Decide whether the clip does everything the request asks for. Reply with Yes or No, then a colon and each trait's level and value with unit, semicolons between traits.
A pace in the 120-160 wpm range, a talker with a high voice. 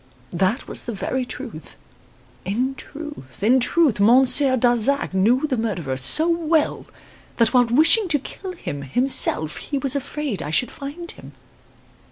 Yes: average, 150 wpm; very high, 255 Hz